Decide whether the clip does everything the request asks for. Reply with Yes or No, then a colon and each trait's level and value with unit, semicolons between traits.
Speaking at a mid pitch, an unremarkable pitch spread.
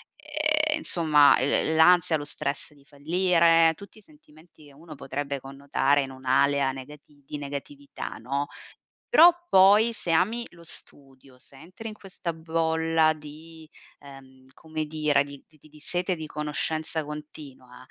Yes: medium, 155 Hz; average, 3.1 semitones